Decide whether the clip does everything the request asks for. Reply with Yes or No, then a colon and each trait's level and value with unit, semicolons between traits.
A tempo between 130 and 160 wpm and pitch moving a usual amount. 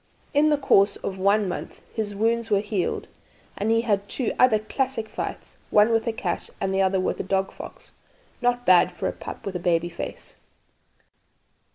No: average, 190 wpm; average, 3.1 semitones